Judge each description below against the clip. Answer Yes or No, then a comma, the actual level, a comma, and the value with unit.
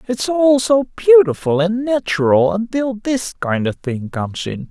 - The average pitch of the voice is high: Yes, high, 205 Hz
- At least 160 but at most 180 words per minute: Yes, average, 165 wpm